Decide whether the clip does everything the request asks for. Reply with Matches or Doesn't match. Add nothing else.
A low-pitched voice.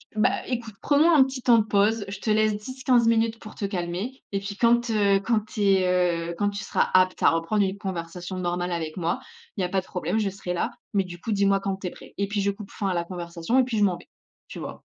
Doesn't match